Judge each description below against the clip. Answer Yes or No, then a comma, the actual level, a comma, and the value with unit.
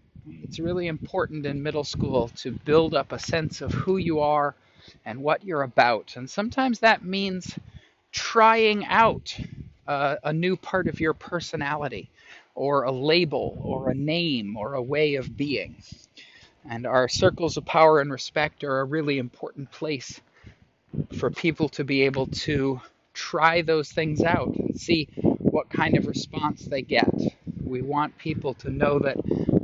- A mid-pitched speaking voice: Yes, medium, 150 Hz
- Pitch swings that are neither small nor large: Yes, average, 3.4 semitones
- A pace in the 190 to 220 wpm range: No, average, 160 wpm